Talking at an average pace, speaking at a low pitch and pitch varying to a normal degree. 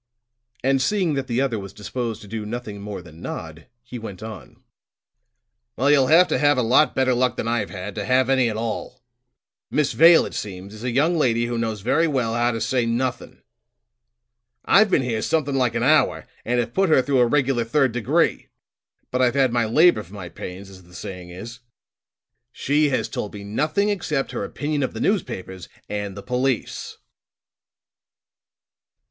Yes: average, 190 wpm; low, 120 Hz; average, 4.4 semitones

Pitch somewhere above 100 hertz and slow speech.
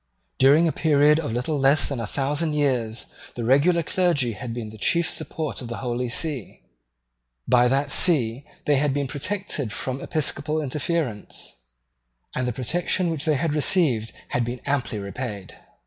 No: medium, 140 Hz; average, 165 wpm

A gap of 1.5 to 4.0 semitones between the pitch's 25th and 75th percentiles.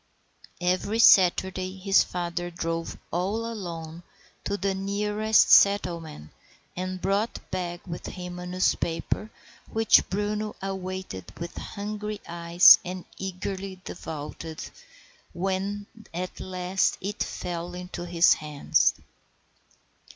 Yes: narrow, 2.5 semitones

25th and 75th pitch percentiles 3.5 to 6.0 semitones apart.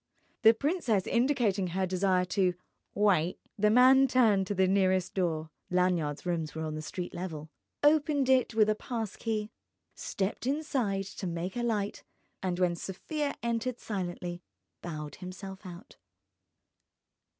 Yes: average, 4.4 semitones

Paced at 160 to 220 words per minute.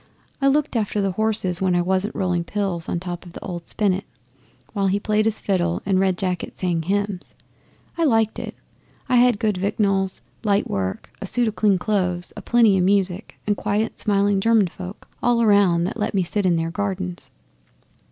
Yes: average, 190 wpm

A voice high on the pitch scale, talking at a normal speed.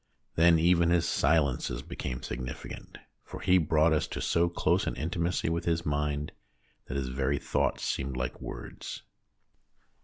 No: very low, 75 Hz; average, 150 wpm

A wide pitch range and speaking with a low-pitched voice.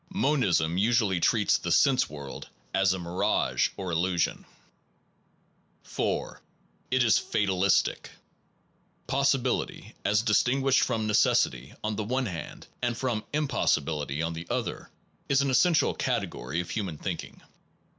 Yes: wide, 6.9 semitones; low, 105 Hz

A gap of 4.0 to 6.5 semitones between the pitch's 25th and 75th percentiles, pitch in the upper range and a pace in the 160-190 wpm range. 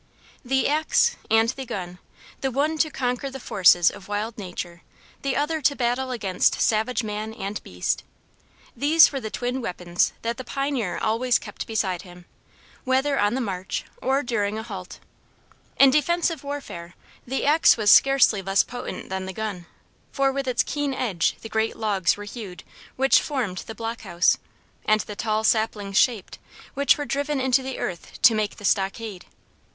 Yes: average, 5.1 semitones; high, 225 Hz; average, 170 wpm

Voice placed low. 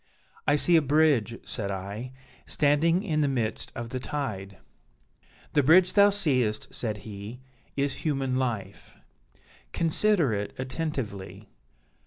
Yes: low, 130 Hz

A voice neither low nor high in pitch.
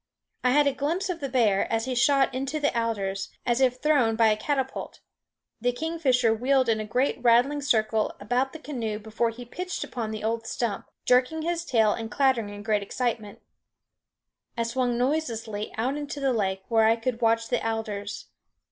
No: high, 240 Hz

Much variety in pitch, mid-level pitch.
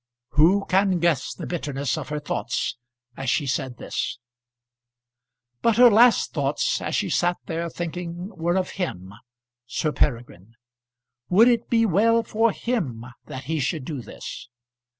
Yes: wide, 6.7 semitones; medium, 170 Hz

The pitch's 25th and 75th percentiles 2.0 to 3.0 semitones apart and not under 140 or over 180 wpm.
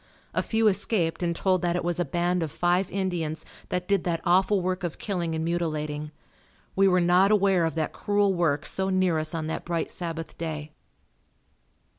No: narrow, 2.5 semitones; average, 190 wpm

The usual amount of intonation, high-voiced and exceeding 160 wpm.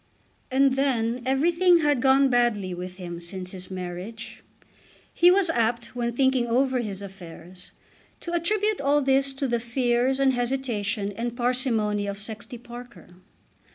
No: average, 4.7 semitones; high, 240 Hz; average, 145 wpm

